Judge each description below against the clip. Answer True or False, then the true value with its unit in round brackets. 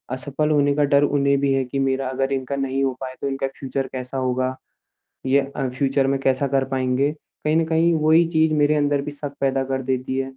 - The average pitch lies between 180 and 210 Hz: False (135 Hz)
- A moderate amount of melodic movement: False (1.5 semitones)